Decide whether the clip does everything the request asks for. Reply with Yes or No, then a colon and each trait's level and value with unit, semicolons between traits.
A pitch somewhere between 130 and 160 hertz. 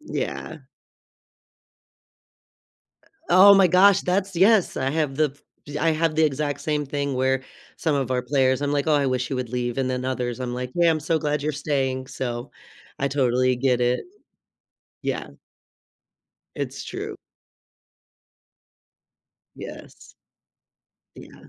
Yes: medium, 140 Hz